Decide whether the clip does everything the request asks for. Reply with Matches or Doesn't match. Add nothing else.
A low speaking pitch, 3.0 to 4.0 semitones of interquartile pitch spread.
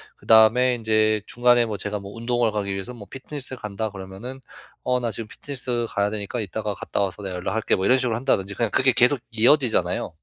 Matches